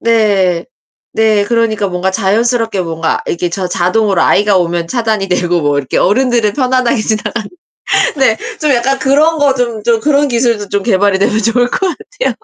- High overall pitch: Yes, high, 220 Hz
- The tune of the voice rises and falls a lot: No, average, 4.3 semitones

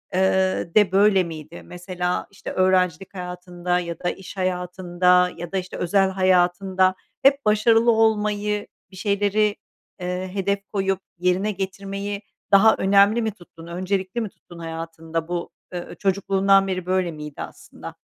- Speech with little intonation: Yes, narrow, 2.0 semitones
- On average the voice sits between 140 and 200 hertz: Yes, medium, 185 Hz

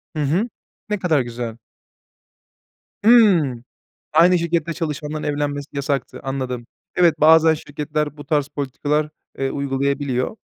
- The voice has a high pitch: No, medium, 150 Hz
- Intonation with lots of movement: No, average, 2.9 semitones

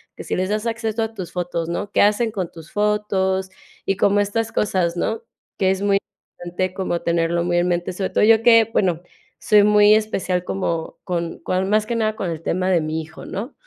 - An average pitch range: Yes, average, 3.3 semitones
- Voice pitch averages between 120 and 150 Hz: No, high, 190 Hz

